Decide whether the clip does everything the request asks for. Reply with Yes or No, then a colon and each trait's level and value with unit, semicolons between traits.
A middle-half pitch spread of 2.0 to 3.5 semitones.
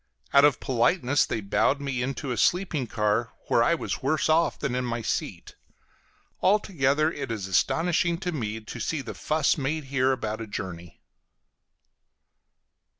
No: wide, 5.5 semitones